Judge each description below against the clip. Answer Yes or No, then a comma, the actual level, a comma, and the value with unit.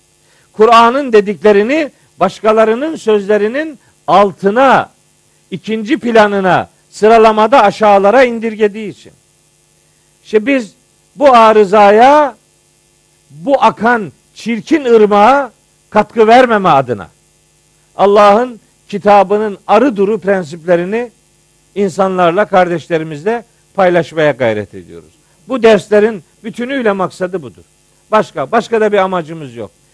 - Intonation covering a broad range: No, average, 3.8 semitones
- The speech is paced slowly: Yes, slow, 85 wpm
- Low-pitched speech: No, high, 210 Hz